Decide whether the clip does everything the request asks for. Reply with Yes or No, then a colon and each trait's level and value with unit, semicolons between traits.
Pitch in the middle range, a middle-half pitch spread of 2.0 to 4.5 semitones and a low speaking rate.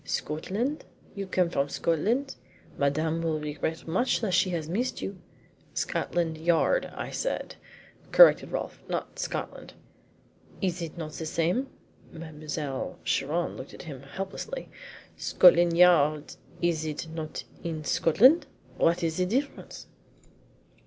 Yes: medium, 170 Hz; average, 3.5 semitones; slow, 125 wpm